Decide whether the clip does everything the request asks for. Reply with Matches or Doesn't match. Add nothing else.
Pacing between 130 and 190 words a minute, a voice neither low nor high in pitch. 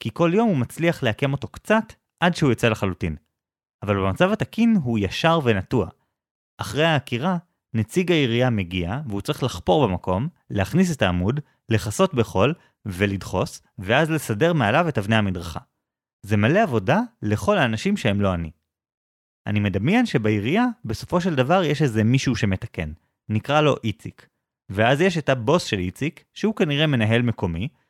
Doesn't match